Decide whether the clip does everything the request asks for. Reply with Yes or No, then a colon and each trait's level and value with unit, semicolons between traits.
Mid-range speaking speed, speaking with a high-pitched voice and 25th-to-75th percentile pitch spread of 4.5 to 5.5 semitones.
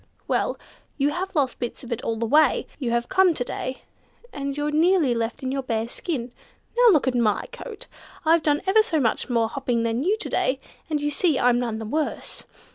No: fast, 215 wpm; very high, 275 Hz; average, 5.0 semitones